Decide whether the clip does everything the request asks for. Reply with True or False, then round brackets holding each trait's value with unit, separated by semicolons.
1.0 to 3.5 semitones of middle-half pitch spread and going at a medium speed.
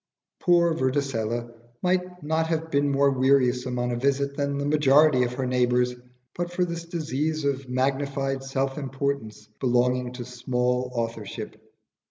True (2.9 semitones; 145 wpm)